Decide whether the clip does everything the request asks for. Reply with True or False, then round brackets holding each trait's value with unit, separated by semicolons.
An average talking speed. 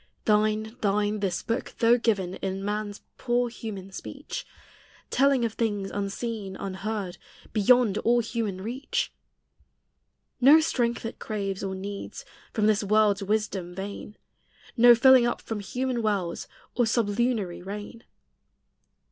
False (125 wpm)